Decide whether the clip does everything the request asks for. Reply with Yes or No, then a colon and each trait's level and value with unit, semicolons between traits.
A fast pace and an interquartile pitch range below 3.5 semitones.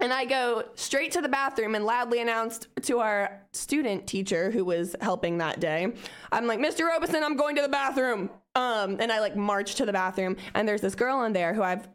No: fast, 220 wpm; average, 5.2 semitones